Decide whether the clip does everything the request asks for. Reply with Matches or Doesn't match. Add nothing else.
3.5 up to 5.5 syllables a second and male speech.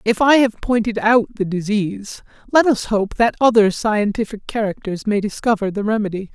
Matches